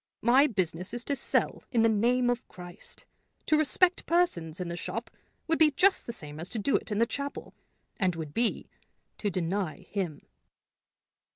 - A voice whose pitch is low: No, high, 225 Hz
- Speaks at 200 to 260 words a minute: No, average, 180 wpm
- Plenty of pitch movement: Yes, wide, 7.4 semitones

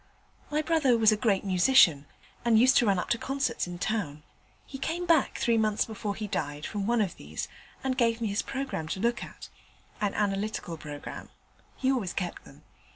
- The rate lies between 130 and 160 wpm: No, average, 195 wpm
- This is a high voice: Yes, high, 215 Hz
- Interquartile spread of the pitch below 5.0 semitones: No, wide, 5.5 semitones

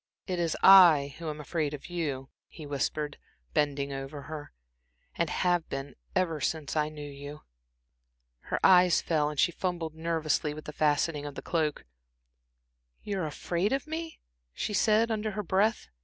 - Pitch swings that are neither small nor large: Yes, average, 3.7 semitones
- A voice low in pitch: No, medium, 155 Hz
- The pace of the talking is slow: No, average, 170 wpm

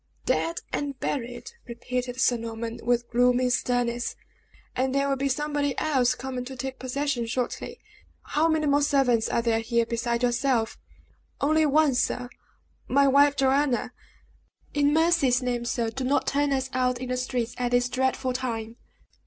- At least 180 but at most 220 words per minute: No, average, 160 wpm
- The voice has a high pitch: Yes, very high, 255 Hz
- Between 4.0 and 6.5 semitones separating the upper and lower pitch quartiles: No, narrow, 2.5 semitones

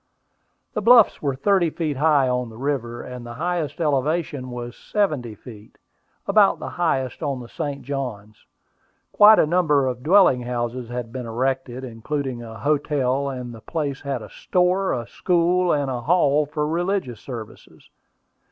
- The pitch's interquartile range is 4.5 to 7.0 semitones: Yes, average, 4.8 semitones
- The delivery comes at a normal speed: Yes, average, 160 wpm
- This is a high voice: No, low, 135 Hz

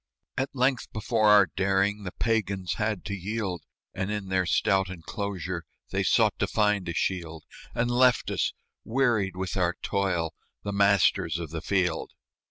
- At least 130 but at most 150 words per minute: No, average, 160 wpm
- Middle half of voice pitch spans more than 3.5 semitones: No, narrow, 2.6 semitones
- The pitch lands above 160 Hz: No, low, 100 Hz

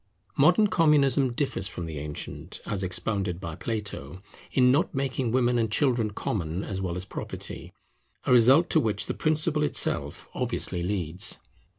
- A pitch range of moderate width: No, wide, 6.9 semitones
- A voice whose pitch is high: No, low, 110 Hz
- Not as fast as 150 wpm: No, average, 155 wpm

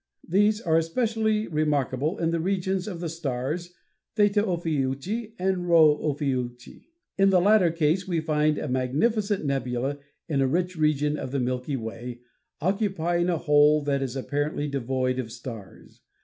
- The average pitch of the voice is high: No, medium, 155 Hz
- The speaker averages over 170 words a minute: No, average, 150 wpm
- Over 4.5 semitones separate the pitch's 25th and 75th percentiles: Yes, average, 5.2 semitones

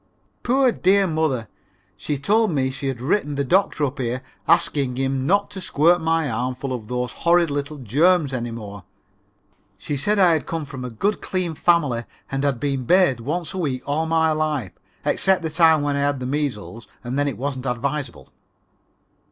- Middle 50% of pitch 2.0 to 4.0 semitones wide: No, average, 4.5 semitones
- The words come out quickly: No, average, 185 wpm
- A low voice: No, medium, 145 Hz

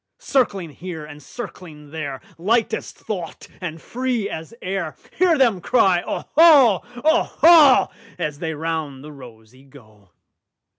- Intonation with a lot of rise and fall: Yes, wide, 8.0 semitones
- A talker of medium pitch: Yes, medium, 170 Hz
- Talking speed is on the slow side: Yes, slow, 110 wpm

